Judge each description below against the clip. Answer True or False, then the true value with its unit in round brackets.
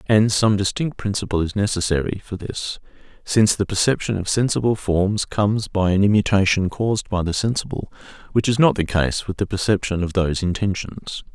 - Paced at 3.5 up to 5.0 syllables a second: False (5.5 syllables/s)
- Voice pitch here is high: False (100 Hz)